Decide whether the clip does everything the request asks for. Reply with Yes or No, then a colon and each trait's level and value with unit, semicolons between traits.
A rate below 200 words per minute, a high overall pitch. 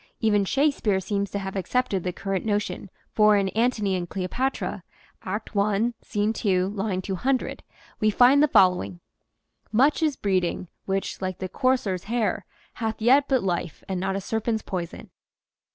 Yes: average, 160 wpm; high, 205 Hz